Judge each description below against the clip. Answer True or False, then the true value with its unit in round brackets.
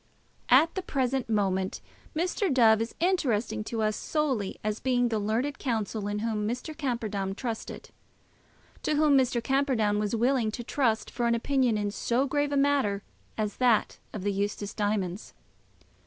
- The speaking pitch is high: True (230 Hz)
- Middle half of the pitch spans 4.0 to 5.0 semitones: True (4.3 semitones)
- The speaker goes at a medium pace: True (160 wpm)